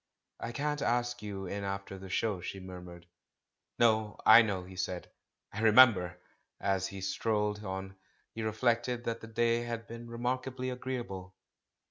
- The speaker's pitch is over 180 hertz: No, low, 110 Hz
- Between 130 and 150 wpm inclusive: No, average, 160 wpm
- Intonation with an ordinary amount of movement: Yes, average, 3.5 semitones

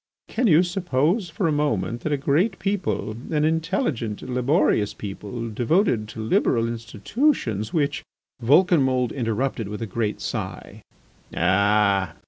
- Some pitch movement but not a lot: No, wide, 7.1 semitones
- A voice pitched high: No, low, 125 Hz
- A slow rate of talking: Yes, slow, 130 wpm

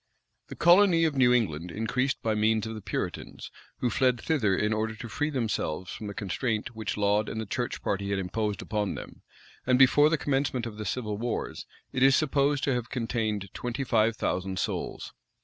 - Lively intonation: No, average, 3.7 semitones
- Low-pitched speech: Yes, low, 115 Hz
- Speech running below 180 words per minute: No, average, 200 wpm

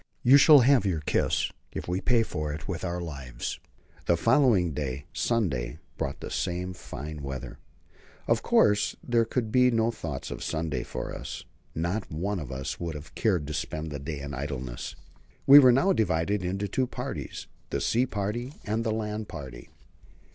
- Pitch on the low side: Yes, very low, 90 Hz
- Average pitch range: No, wide, 7.2 semitones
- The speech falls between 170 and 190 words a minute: Yes, average, 180 wpm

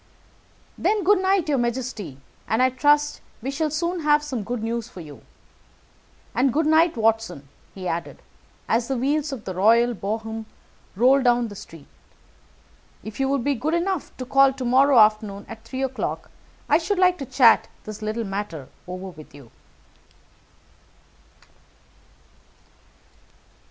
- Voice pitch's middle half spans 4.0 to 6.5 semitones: Yes, average, 5.3 semitones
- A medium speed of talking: Yes, average, 150 wpm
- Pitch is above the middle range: Yes, high, 245 Hz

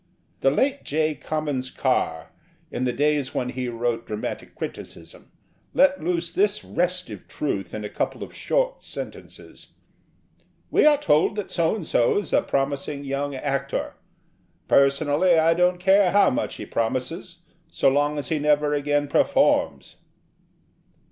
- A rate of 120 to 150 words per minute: Yes, average, 145 wpm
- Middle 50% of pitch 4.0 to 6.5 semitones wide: Yes, average, 4.7 semitones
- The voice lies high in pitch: No, medium, 150 Hz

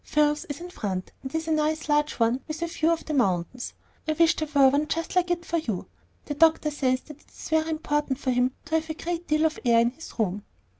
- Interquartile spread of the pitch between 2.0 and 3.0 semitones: No, average, 3.8 semitones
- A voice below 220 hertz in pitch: No, very high, 300 Hz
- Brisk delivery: Yes, fast, 250 wpm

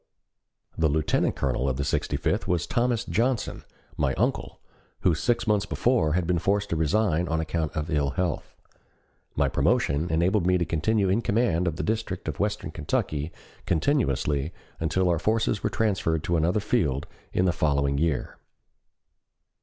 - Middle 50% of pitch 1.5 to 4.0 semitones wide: No, average, 5.1 semitones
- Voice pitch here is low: Yes, very low, 85 Hz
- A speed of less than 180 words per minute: Yes, average, 160 wpm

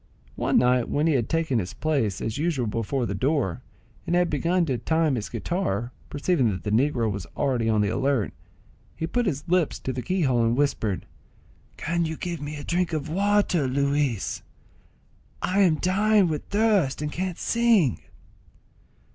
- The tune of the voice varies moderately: No, wide, 6.3 semitones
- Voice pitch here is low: No, medium, 145 Hz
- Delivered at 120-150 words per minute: No, average, 175 wpm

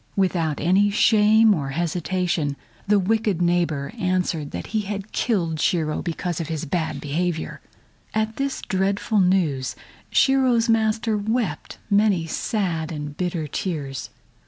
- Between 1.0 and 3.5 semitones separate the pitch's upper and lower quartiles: No, average, 4.8 semitones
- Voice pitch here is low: No, medium, 180 Hz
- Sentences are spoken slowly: Yes, slow, 130 wpm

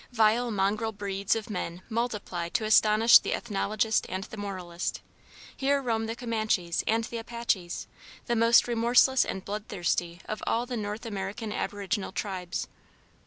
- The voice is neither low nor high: No, high, 215 Hz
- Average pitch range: Yes, average, 3.0 semitones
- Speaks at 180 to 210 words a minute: No, average, 145 wpm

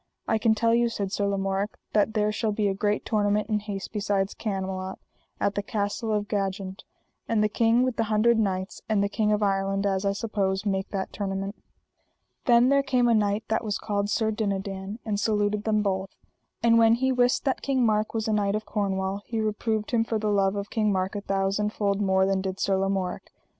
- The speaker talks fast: Yes, fast, 215 wpm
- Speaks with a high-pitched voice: Yes, high, 205 Hz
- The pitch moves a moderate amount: No, narrow, 1.9 semitones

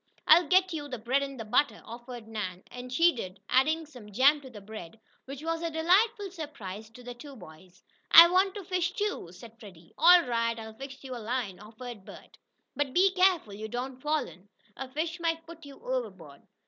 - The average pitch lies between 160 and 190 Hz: No, very high, 265 Hz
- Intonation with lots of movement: Yes, wide, 6.9 semitones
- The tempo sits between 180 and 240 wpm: Yes, average, 200 wpm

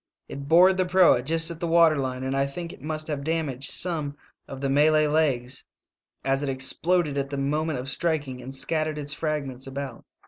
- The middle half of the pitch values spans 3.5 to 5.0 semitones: No, average, 3.0 semitones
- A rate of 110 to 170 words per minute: No, fast, 205 wpm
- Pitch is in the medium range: Yes, medium, 145 Hz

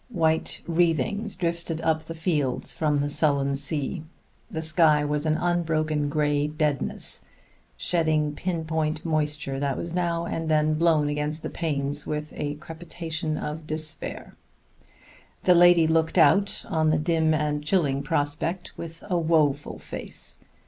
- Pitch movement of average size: No, narrow, 2.0 semitones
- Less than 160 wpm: Yes, average, 140 wpm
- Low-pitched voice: No, medium, 155 Hz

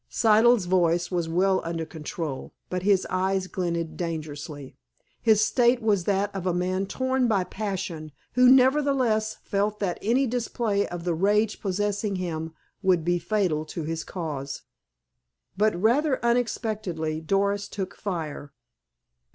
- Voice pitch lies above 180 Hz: Yes, high, 190 Hz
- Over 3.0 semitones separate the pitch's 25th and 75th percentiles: Yes, average, 4.3 semitones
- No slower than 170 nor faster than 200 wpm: No, slow, 135 wpm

